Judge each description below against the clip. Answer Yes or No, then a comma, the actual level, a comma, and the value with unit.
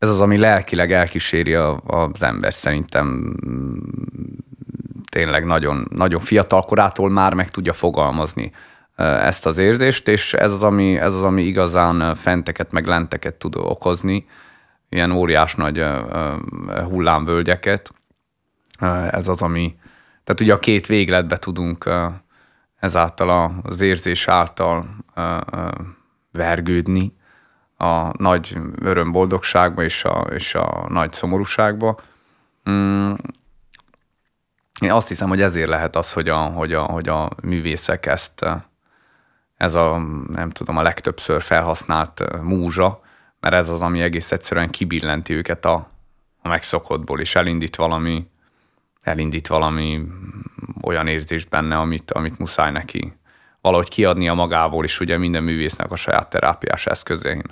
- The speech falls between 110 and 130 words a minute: Yes, average, 120 wpm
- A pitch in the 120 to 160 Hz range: No, very low, 85 Hz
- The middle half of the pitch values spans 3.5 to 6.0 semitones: No, narrow, 2.5 semitones